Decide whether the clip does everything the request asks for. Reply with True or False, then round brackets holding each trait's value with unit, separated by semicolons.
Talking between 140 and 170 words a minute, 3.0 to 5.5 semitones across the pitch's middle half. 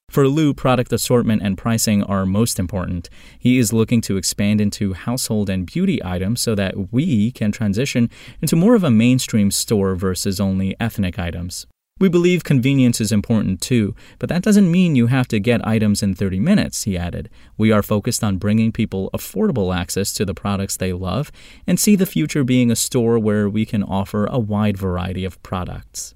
False (190 wpm; 4.2 semitones)